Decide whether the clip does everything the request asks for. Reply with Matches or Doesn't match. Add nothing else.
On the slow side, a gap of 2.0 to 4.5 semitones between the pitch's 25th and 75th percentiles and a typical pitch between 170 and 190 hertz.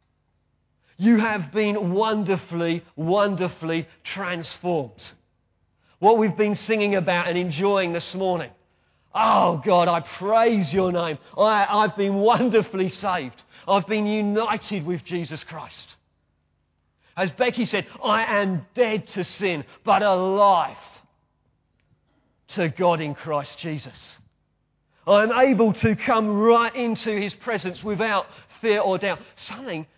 Doesn't match